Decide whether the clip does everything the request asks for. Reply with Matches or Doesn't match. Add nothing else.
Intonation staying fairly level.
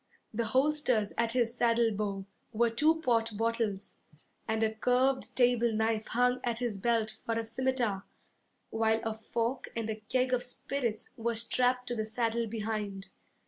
Matches